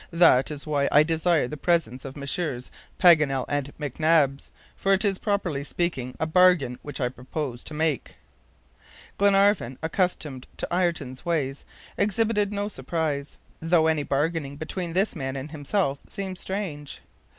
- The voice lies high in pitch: No, medium, 155 Hz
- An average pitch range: Yes, average, 4.5 semitones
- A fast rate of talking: No, average, 145 wpm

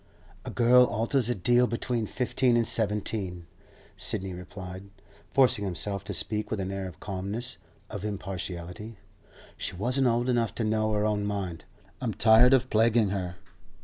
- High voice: No, low, 105 Hz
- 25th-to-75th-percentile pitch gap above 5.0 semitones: No, average, 3.6 semitones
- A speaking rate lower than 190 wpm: Yes, average, 155 wpm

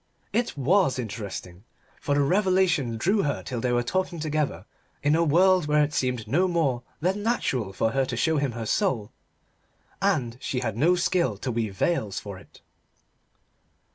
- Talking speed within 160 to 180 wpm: Yes, average, 170 wpm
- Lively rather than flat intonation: Yes, wide, 7.1 semitones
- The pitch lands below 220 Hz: Yes, medium, 140 Hz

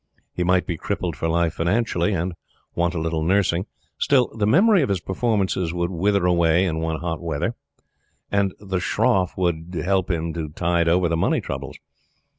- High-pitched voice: No, very low, 90 Hz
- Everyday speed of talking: Yes, average, 180 wpm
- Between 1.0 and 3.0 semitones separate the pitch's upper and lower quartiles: Yes, average, 2.7 semitones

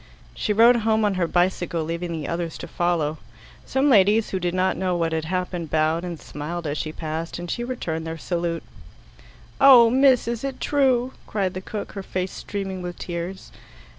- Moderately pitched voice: Yes, medium, 180 Hz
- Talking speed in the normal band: Yes, average, 190 wpm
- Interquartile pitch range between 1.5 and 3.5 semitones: No, average, 4.5 semitones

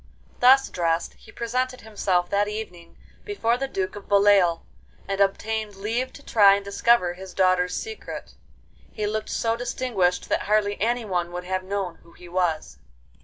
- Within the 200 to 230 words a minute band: No, average, 160 wpm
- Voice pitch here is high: Yes, high, 200 Hz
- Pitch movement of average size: Yes, average, 3.9 semitones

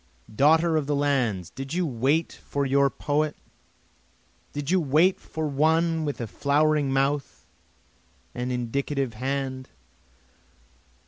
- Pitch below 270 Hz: Yes, medium, 140 Hz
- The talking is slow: Yes, slow, 120 wpm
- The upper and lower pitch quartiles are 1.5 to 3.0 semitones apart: Yes, narrow, 2.5 semitones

